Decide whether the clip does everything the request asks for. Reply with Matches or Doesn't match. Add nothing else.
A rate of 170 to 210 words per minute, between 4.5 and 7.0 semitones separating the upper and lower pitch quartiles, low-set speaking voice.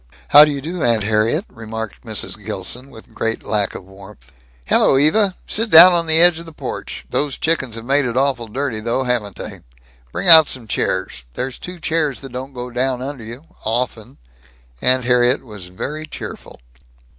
Matches